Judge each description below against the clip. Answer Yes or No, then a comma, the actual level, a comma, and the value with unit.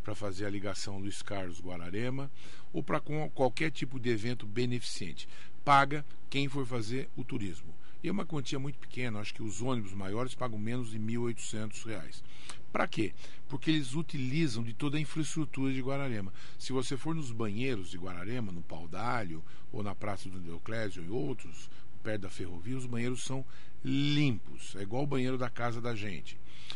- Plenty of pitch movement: No, average, 4.9 semitones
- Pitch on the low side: Yes, low, 125 Hz